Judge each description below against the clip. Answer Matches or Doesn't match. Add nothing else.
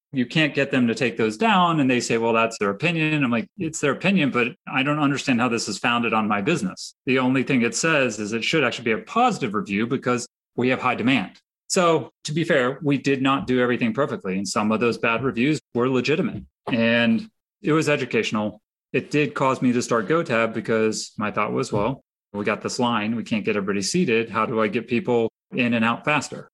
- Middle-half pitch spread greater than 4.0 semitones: Matches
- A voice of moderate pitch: Doesn't match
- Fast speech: Matches